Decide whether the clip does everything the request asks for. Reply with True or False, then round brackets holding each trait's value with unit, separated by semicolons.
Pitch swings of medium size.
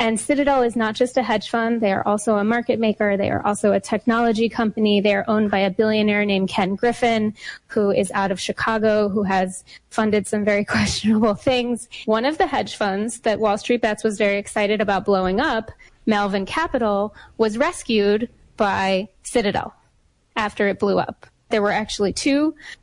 False (2.1 semitones)